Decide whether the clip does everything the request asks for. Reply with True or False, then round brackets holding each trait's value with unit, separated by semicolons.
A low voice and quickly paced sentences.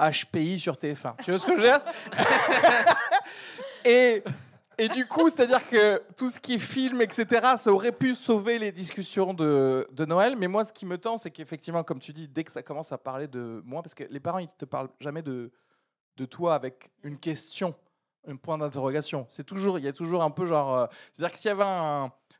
False (175 Hz; 225 wpm)